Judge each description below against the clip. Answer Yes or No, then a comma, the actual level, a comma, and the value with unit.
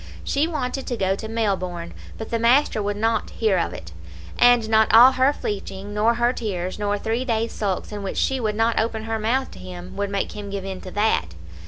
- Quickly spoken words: Yes, fast, 220 wpm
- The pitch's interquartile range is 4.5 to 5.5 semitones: No, average, 2.9 semitones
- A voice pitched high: Yes, high, 220 Hz